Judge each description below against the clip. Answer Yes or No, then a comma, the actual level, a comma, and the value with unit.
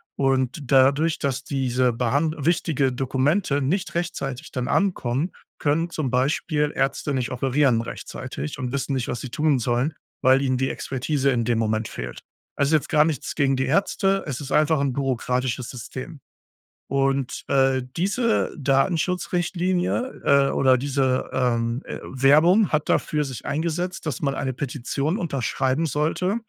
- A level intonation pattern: No, average, 3.3 semitones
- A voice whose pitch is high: No, medium, 140 Hz